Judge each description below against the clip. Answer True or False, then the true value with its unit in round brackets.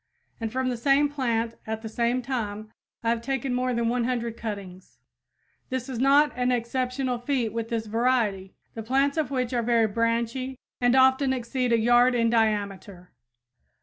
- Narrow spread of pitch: True (2.3 semitones)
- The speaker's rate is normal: True (170 wpm)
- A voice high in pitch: True (240 Hz)